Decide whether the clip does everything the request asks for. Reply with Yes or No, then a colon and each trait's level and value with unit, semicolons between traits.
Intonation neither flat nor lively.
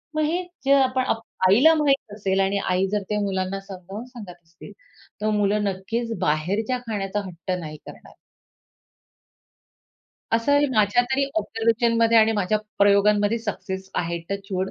Yes: average, 3.2 semitones